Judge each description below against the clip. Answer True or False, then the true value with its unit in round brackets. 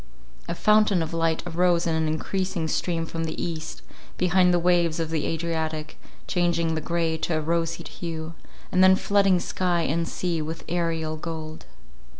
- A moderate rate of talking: True (165 wpm)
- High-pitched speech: False (165 Hz)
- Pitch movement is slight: True (1.7 semitones)